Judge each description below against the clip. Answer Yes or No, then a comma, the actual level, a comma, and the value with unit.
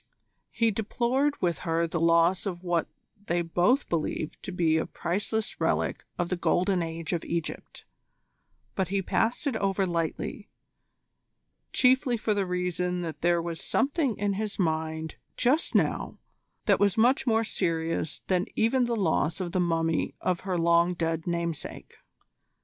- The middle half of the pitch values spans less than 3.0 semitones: No, average, 4.3 semitones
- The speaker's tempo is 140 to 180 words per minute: Yes, average, 155 wpm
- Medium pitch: Yes, medium, 180 Hz